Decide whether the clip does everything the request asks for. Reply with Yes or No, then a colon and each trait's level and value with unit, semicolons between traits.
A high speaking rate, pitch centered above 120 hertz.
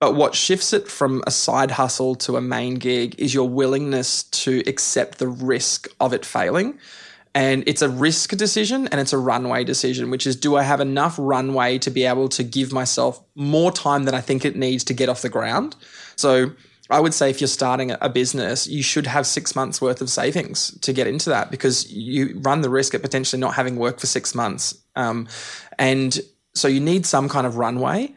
Yes: fast, 215 wpm; low, 135 Hz